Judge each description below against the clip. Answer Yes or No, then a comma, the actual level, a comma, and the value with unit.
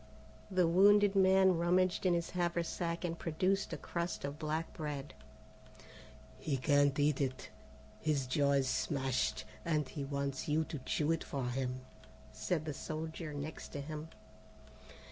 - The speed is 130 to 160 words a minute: Yes, average, 145 wpm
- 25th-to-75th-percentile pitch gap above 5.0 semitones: No, average, 3.4 semitones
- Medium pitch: Yes, medium, 155 Hz